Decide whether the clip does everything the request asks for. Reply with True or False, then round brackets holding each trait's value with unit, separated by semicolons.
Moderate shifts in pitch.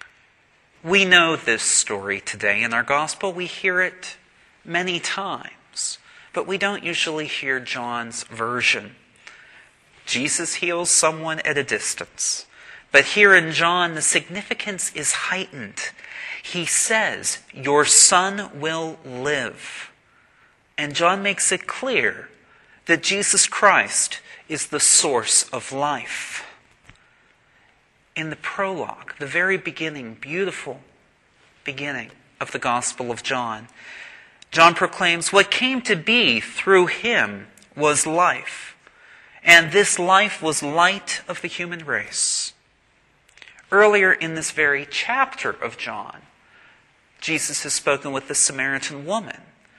True (4.9 semitones)